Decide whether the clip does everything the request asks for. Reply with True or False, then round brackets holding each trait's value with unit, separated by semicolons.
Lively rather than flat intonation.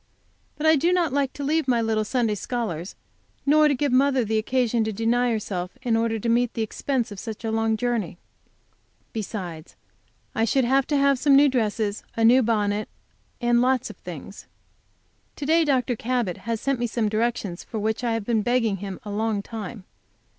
False (3.2 semitones)